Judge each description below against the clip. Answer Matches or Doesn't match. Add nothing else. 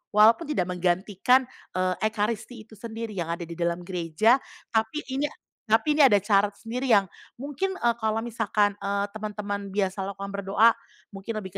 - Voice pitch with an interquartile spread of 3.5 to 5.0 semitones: Doesn't match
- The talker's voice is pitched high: Matches